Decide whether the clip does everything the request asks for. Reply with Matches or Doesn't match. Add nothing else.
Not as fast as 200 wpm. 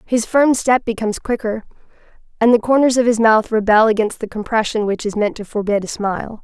Doesn't match